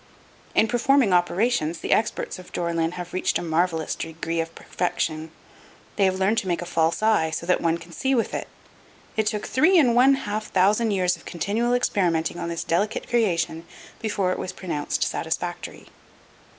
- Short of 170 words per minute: No, average, 180 wpm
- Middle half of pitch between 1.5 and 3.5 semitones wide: No, average, 4.6 semitones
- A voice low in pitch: No, medium, 185 Hz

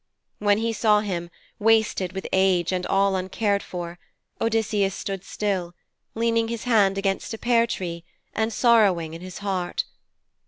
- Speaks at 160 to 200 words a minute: No, average, 150 wpm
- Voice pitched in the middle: No, high, 200 Hz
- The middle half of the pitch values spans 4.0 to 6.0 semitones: No, average, 3.3 semitones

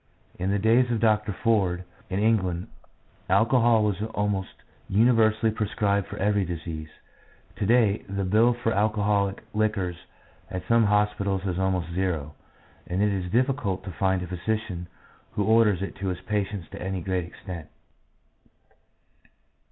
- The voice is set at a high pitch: No, low, 100 Hz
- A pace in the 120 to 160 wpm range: Yes, average, 145 wpm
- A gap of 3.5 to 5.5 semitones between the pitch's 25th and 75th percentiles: No, average, 2.8 semitones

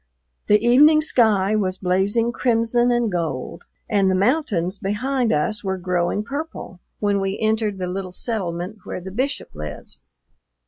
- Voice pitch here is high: Yes, high, 205 Hz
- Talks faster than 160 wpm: No, average, 145 wpm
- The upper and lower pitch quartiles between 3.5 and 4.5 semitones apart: Yes, average, 4.2 semitones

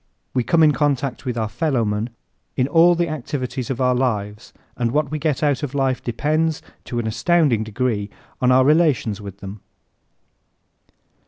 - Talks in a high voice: No, low, 130 Hz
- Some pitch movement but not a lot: Yes, average, 4.8 semitones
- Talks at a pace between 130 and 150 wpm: No, average, 165 wpm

